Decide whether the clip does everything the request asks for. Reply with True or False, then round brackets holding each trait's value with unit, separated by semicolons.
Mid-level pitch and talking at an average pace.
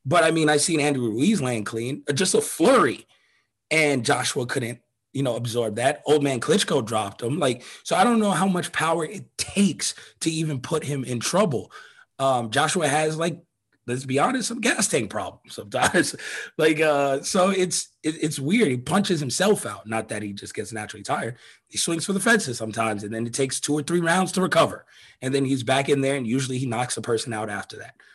False (145 Hz; 215 wpm)